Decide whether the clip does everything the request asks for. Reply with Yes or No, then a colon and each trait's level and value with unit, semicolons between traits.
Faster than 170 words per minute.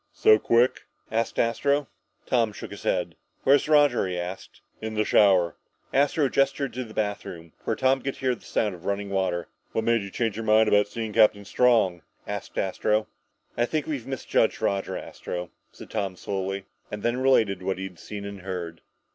Yes: average, 185 wpm